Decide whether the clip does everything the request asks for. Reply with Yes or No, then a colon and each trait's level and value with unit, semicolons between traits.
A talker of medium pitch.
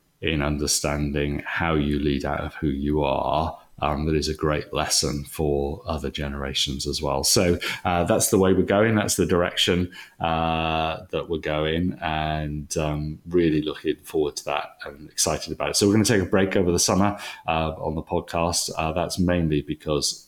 No: very low, 80 Hz